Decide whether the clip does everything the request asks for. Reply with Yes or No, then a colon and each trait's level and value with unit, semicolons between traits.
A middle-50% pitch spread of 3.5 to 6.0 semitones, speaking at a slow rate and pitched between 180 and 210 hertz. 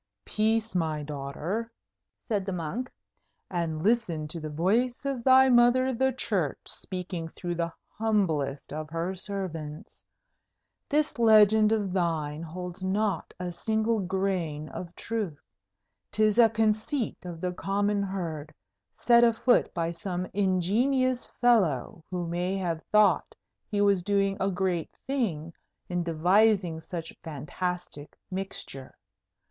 Yes: average, 4.8 semitones; slow, 125 wpm; high, 190 Hz